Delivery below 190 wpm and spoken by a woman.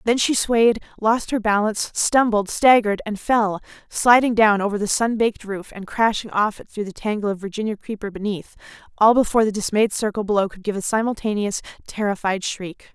Yes: average, 180 wpm; female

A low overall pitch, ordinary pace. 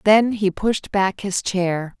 No: high, 195 Hz; average, 180 wpm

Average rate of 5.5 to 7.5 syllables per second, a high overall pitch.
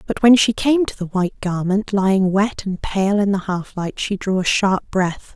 No: 4.7 syllables/s; high, 195 Hz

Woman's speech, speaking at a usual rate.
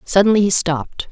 Yes: female; average, 160 wpm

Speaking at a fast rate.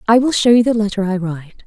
Yes: fast, 290 wpm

